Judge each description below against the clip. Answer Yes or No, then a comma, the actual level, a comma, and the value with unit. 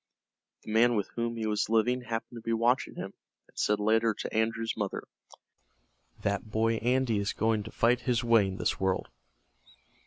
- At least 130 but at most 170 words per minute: No, average, 180 wpm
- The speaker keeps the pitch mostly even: Yes, narrow, 1.8 semitones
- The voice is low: Yes, low, 115 Hz